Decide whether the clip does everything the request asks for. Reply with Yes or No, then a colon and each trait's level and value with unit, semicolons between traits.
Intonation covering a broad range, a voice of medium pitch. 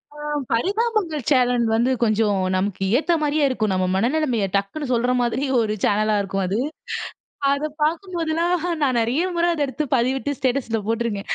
No: wide, 6.0 semitones; very high, 250 Hz